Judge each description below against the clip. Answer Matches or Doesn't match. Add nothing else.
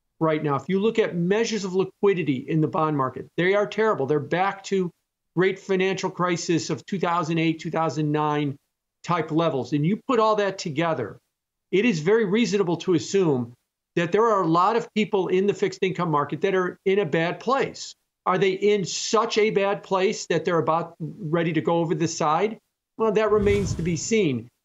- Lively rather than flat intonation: Doesn't match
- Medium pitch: Matches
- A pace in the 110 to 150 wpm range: Doesn't match